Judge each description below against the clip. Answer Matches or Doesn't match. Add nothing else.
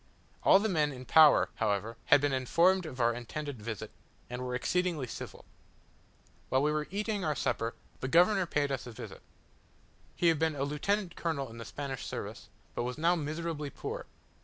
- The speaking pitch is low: Doesn't match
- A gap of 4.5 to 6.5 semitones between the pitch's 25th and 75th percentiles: Matches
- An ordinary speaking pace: Matches